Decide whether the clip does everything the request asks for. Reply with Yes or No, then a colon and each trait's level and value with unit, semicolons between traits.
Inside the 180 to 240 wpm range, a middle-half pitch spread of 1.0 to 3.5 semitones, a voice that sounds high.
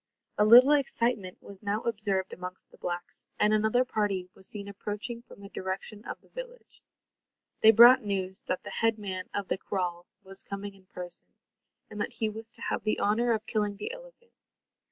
Yes: average, 190 wpm; average, 3.0 semitones; high, 210 Hz